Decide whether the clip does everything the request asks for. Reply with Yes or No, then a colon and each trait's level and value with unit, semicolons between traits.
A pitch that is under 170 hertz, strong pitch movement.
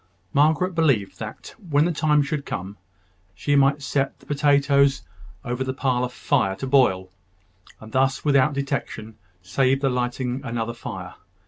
No: low, 135 Hz; average, 2.8 semitones